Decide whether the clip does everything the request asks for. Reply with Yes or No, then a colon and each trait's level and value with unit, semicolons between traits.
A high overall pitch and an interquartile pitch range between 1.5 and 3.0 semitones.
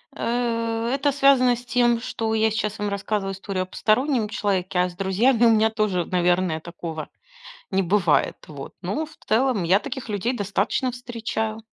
No: high, 215 Hz; average, 4.1 semitones